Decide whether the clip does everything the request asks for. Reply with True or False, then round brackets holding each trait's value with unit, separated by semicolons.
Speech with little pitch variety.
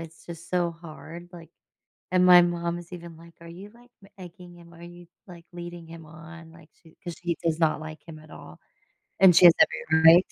True (1.2 semitones)